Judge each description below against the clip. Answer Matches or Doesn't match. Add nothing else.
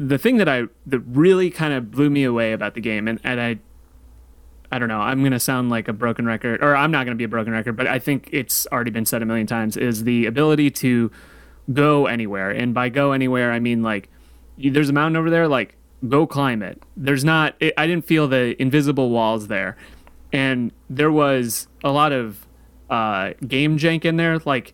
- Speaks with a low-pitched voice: Matches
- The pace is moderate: Doesn't match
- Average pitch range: Matches